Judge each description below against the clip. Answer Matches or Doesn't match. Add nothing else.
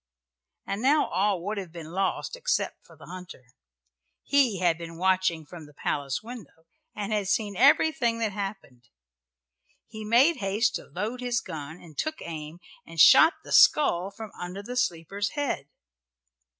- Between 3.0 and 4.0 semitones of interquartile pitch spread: Doesn't match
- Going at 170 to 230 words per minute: Doesn't match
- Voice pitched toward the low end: Doesn't match